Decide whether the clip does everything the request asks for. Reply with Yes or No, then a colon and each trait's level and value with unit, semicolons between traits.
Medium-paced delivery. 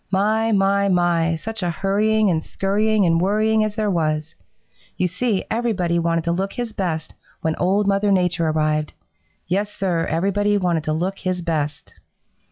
Yes: average, 165 wpm